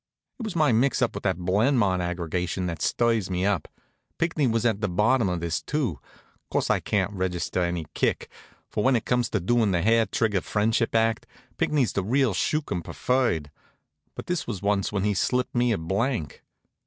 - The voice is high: No, low, 105 Hz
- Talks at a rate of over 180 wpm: Yes, average, 190 wpm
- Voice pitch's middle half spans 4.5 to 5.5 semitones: Yes, average, 4.9 semitones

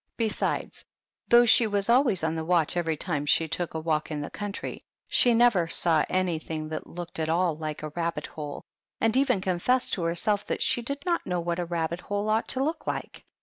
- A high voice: No, medium, 175 Hz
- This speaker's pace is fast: Yes, fast, 210 wpm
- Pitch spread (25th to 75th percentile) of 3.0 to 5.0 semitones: No, wide, 5.4 semitones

